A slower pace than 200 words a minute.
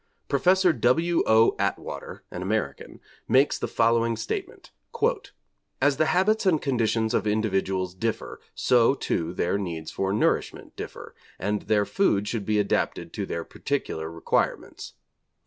Yes: slow, 135 wpm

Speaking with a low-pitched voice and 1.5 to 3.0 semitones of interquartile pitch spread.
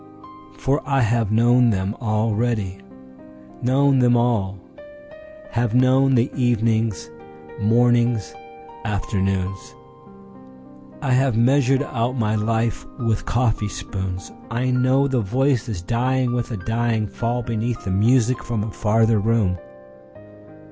No: low, 115 Hz; average, 3.4 semitones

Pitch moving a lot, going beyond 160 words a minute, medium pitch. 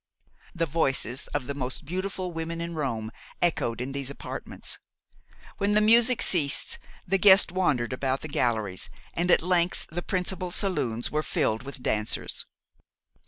No: wide, 6.0 semitones; average, 150 wpm; medium, 160 Hz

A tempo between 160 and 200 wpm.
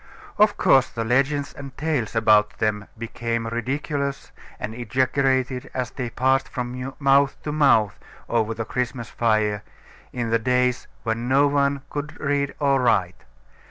No: average, 145 wpm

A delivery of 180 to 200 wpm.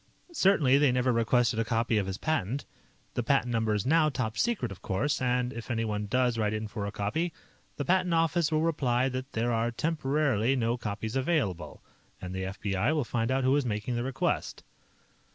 Yes: average, 195 wpm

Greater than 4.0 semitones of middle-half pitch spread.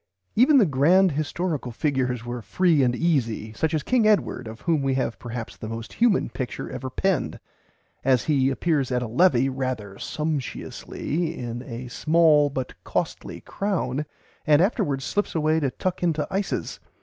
Yes: average, 5.3 semitones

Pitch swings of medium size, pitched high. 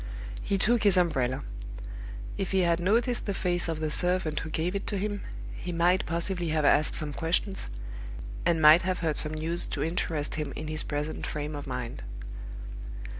No: average, 3.2 semitones; medium, 165 Hz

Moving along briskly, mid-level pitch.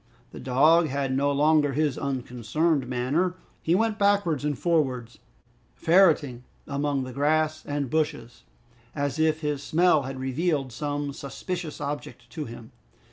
No: slow, 135 wpm; medium, 145 Hz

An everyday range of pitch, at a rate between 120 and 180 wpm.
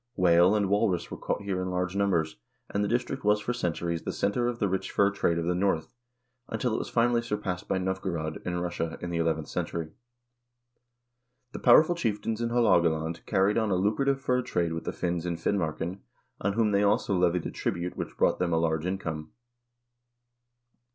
No: average, 3.6 semitones; average, 195 wpm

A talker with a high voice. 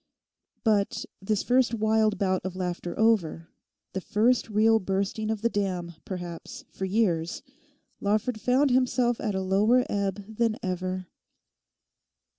Yes: high, 205 Hz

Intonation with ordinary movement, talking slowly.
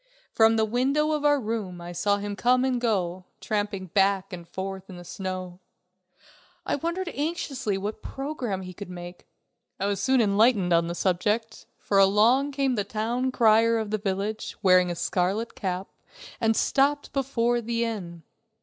No: average, 4.4 semitones; average, 170 wpm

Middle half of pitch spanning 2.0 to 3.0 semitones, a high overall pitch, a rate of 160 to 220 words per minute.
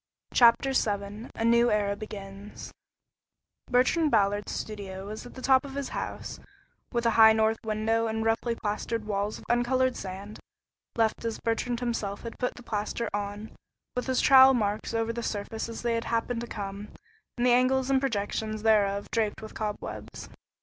Yes: narrow, 2.5 semitones; high, 225 Hz; average, 170 wpm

